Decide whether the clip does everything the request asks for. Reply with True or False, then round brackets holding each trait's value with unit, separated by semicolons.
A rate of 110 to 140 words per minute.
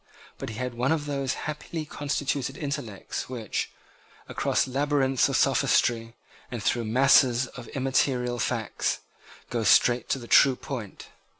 True (135 wpm)